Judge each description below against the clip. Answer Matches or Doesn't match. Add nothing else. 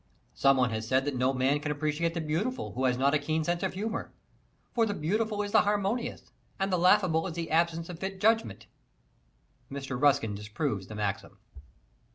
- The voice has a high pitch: Doesn't match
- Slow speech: Doesn't match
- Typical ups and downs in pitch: Doesn't match